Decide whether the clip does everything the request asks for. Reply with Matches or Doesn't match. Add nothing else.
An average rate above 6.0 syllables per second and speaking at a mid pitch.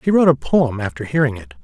Doesn't match